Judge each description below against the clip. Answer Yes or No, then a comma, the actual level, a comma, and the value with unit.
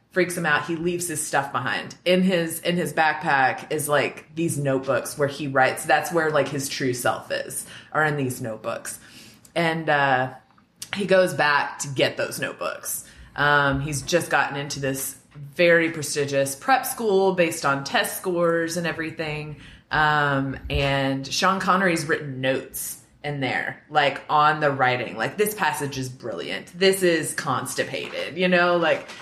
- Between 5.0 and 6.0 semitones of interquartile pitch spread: No, average, 3.7 semitones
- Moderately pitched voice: Yes, medium, 150 Hz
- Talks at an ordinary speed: Yes, average, 160 wpm